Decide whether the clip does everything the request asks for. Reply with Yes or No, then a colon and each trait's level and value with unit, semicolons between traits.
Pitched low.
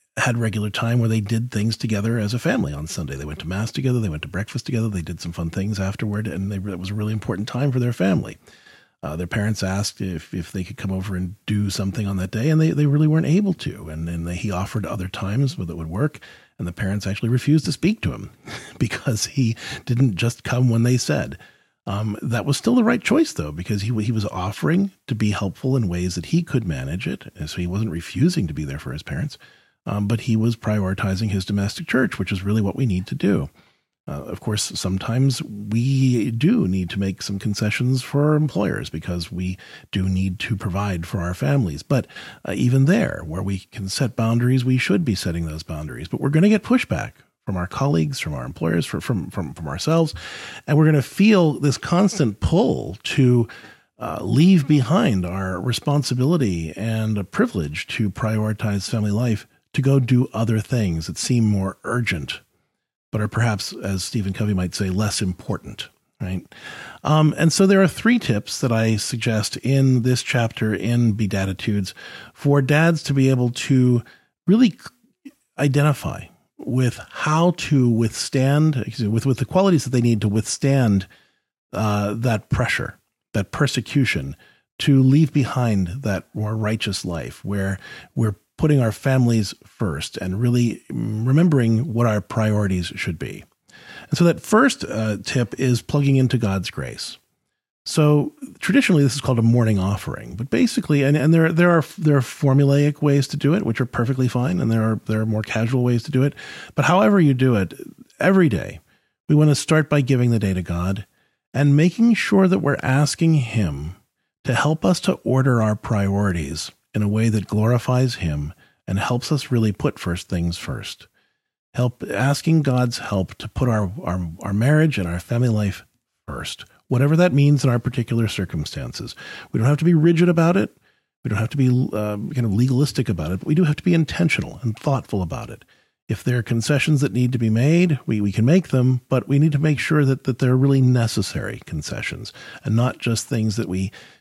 Yes: low, 115 Hz